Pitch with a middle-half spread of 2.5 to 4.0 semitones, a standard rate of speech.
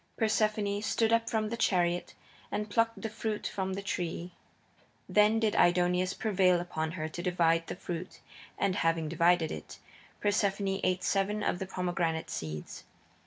Yes: average, 3.2 semitones; average, 155 wpm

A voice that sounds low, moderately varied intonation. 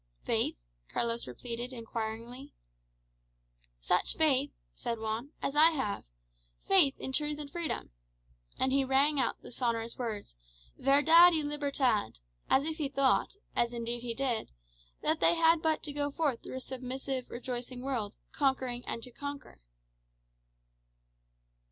No: very high, 265 Hz; average, 3.5 semitones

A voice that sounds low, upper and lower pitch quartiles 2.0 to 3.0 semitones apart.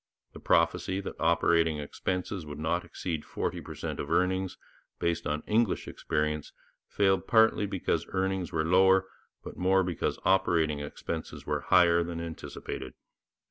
Yes: very low, 85 Hz; average, 2.7 semitones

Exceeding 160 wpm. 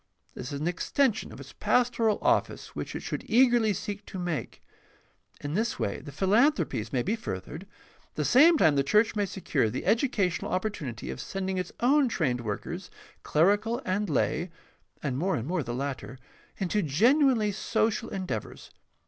Yes: average, 175 wpm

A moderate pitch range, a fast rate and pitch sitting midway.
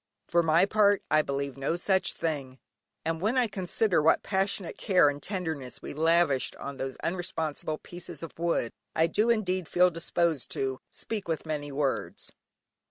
No: average, 4.4 semitones; average, 165 wpm; medium, 165 Hz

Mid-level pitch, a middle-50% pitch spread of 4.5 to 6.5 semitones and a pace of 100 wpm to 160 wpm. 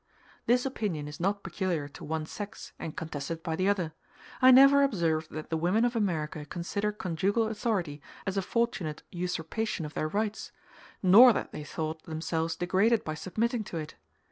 No: medium, 180 Hz; average, 5.3 semitones; average, 170 wpm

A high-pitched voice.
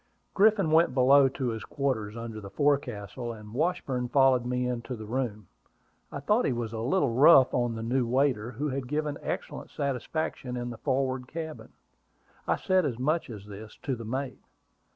No: low, 125 Hz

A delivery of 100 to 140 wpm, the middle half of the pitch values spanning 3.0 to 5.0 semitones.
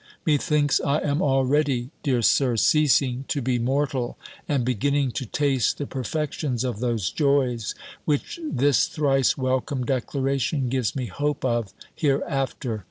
No: slow, 135 wpm; narrow, 2.5 semitones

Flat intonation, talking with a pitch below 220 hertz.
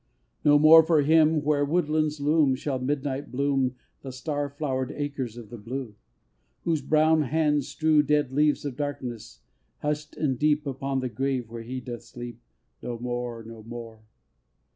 No: average, 3.2 semitones; medium, 140 Hz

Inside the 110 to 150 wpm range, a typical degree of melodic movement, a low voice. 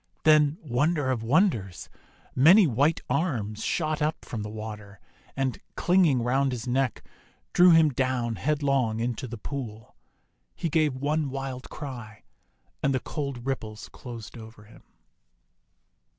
Yes: slow, 135 wpm; average, 4.7 semitones; low, 130 Hz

